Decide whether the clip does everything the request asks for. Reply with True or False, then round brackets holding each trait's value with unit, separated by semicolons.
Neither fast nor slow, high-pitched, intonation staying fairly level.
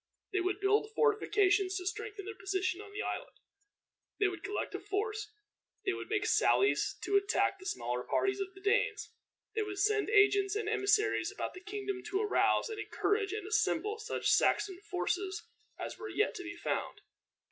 True (180 wpm; 400 Hz; 1.7 semitones)